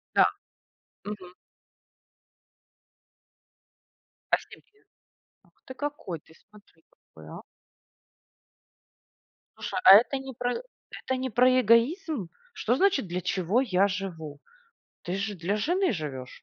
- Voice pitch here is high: Yes, high, 210 Hz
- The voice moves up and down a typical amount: No, wide, 6.4 semitones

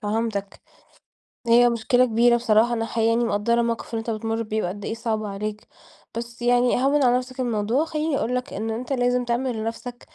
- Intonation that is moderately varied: No, narrow, 1.8 semitones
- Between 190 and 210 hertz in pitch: No, high, 235 Hz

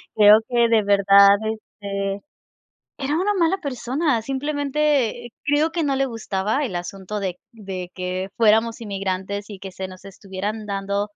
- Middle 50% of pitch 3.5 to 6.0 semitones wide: Yes, average, 5.2 semitones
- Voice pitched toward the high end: Yes, high, 210 Hz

